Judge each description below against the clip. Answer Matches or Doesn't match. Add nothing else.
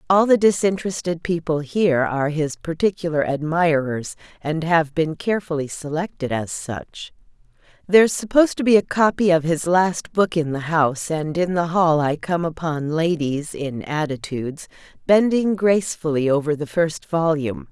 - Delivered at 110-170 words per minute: Matches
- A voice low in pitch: Doesn't match